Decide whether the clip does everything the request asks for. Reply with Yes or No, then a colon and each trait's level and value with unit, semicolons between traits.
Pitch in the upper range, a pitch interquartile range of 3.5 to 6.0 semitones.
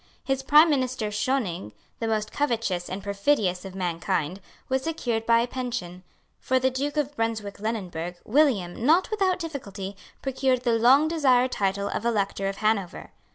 Yes: high, 230 Hz; average, 5.3 semitones